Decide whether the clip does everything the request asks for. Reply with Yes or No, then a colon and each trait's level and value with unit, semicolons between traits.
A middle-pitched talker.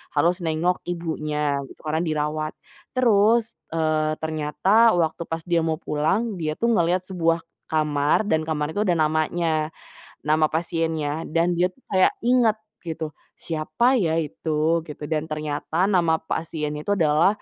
Yes: medium, 160 Hz